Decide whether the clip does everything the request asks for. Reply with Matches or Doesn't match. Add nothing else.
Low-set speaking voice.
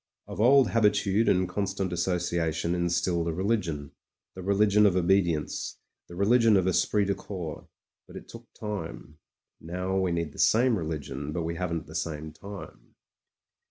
Matches